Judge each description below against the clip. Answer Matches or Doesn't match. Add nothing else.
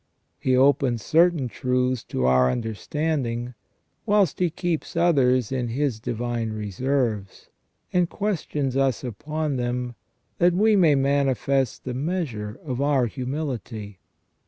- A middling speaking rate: Doesn't match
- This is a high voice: Doesn't match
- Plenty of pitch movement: Doesn't match